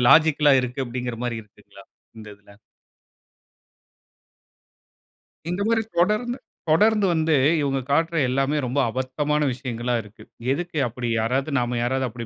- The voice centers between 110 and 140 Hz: Yes, low, 135 Hz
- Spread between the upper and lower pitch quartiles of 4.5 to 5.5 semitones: Yes, average, 4.8 semitones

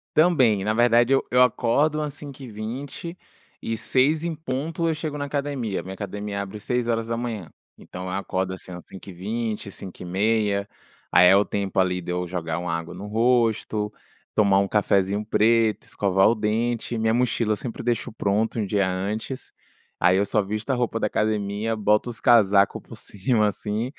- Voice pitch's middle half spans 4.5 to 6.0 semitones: No, average, 3.4 semitones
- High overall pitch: No, low, 110 Hz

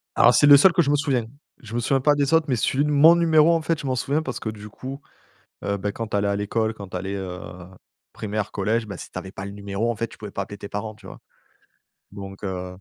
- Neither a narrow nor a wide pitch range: No, wide, 6.0 semitones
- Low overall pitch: Yes, low, 110 Hz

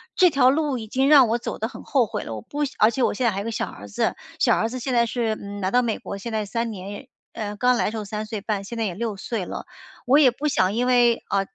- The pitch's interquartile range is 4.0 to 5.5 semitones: No, average, 3.5 semitones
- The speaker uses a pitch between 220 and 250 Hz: Yes, high, 230 Hz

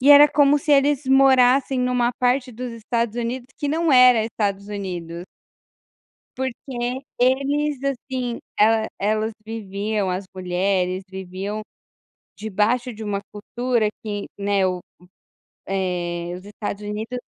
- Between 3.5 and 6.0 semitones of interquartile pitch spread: Yes, average, 4.2 semitones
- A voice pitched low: No, high, 225 Hz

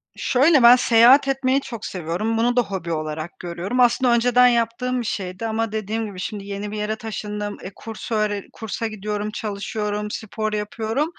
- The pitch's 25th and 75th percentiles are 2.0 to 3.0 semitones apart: Yes, narrow, 2.5 semitones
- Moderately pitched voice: No, high, 220 Hz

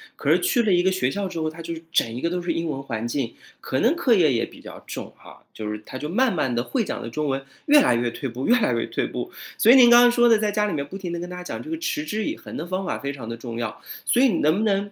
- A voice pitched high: No, medium, 175 Hz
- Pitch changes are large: Yes, wide, 8.5 semitones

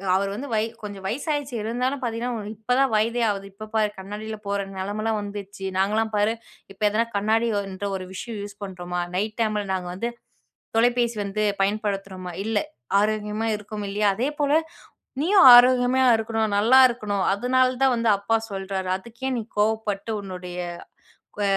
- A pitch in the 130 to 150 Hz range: No, high, 215 Hz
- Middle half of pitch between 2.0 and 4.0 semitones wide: Yes, average, 2.8 semitones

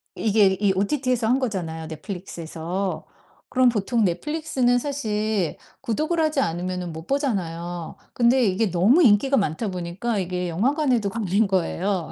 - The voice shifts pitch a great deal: Yes, wide, 5.7 semitones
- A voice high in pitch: Yes, high, 205 Hz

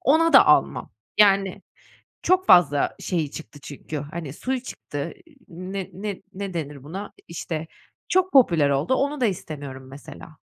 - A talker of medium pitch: Yes, medium, 175 Hz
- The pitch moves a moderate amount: No, wide, 6.4 semitones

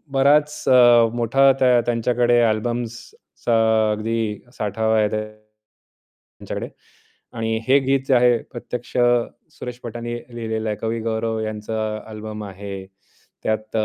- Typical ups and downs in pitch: No, narrow, 1.9 semitones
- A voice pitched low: Yes, low, 115 Hz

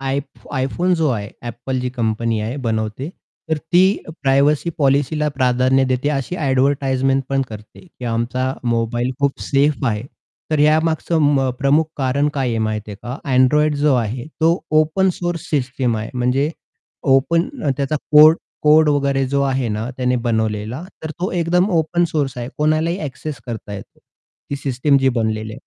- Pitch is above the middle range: No, low, 135 Hz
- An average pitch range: Yes, average, 3.7 semitones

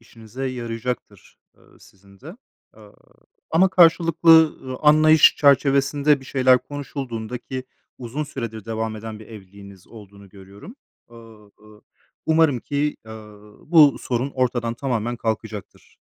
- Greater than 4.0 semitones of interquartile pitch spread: Yes, average, 4.7 semitones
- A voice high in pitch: No, low, 120 Hz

